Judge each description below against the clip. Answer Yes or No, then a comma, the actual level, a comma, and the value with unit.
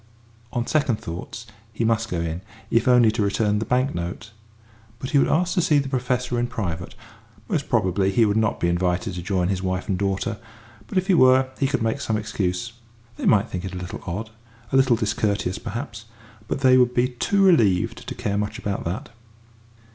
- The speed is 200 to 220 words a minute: Yes, fast, 205 wpm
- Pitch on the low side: Yes, low, 110 Hz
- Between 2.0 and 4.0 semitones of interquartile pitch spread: No, average, 4.8 semitones